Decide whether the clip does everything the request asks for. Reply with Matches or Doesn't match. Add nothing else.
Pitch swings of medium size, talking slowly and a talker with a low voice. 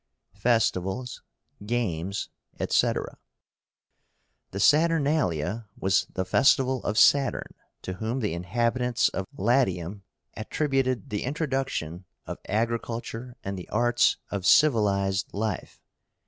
Matches